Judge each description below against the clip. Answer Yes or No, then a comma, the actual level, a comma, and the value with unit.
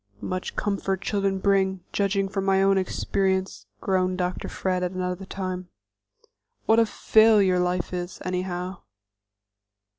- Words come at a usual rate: No, slow, 125 wpm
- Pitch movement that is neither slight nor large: No, narrow, 1.3 semitones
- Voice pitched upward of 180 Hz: Yes, high, 190 Hz